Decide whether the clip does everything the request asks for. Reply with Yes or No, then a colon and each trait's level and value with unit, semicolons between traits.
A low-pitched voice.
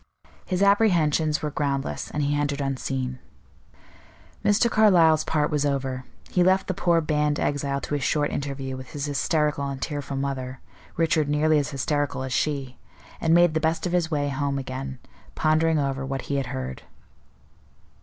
No: medium, 145 Hz